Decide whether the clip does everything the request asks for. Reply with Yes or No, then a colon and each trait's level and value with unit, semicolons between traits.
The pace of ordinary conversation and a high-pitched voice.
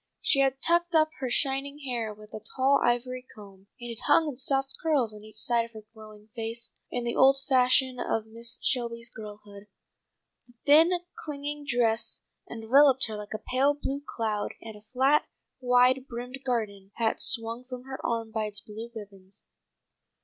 Yes: average, 175 wpm; high, 240 Hz